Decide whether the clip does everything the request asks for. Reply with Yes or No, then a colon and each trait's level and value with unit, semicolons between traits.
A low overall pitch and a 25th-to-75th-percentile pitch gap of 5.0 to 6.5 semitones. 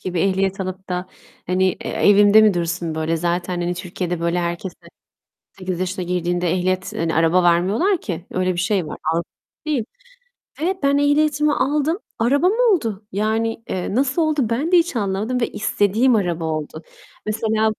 No: high, 190 Hz; average, 5.3 semitones